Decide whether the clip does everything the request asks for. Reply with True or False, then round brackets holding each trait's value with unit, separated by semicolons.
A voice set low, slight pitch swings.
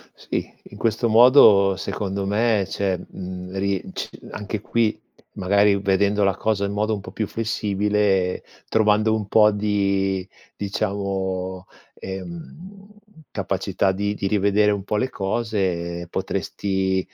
True (100 Hz; 1.8 semitones)